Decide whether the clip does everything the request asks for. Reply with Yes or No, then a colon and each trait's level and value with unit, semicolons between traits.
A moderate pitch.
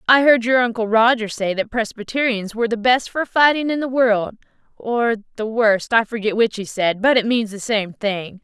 No: high, 225 Hz